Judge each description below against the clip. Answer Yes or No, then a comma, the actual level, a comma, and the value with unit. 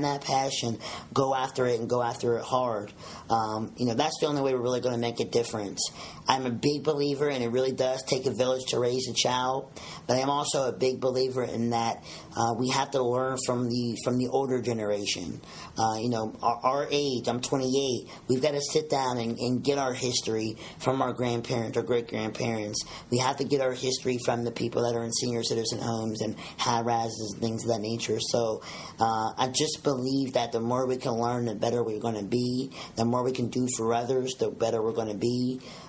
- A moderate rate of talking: No, fast, 225 wpm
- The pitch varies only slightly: Yes, narrow, 2.1 semitones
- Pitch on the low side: Yes, low, 125 Hz